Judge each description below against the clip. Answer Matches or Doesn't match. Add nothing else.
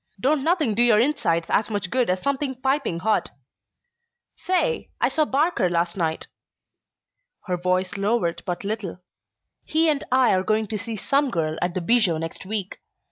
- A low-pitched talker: Doesn't match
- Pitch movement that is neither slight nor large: Doesn't match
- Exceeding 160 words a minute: Matches